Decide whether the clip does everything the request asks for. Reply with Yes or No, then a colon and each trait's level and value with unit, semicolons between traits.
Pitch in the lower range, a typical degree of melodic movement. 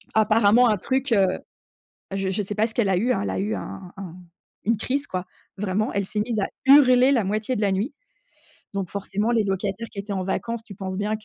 No: high, 210 Hz; average, 3.1 semitones